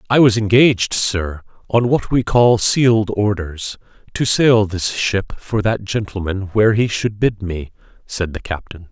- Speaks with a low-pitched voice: Yes, low, 105 Hz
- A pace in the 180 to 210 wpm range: No, average, 170 wpm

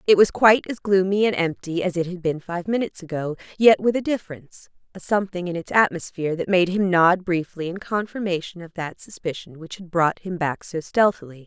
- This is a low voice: No, medium, 180 Hz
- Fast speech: Yes, fast, 210 wpm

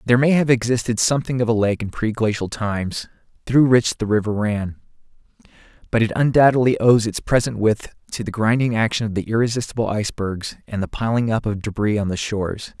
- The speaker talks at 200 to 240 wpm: No, average, 190 wpm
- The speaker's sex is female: No, male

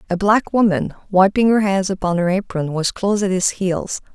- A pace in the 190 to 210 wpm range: Yes, fast, 205 wpm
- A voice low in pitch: No, high, 190 Hz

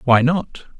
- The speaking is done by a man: Yes, male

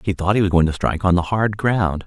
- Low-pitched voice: Yes, very low, 95 Hz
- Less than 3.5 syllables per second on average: No, 6.1 syllables/s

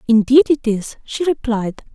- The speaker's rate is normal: Yes, average, 155 wpm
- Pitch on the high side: Yes, high, 245 Hz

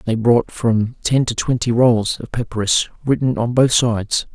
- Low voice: Yes, low, 115 Hz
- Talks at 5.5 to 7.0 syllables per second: No, 4.5 syllables/s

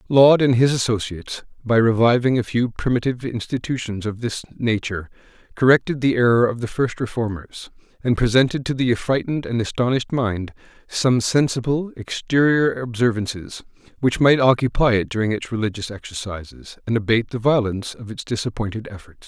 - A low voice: Yes, low, 120 Hz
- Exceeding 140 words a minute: Yes, average, 150 wpm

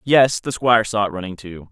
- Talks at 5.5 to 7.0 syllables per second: Yes, 5.6 syllables/s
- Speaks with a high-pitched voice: No, low, 110 Hz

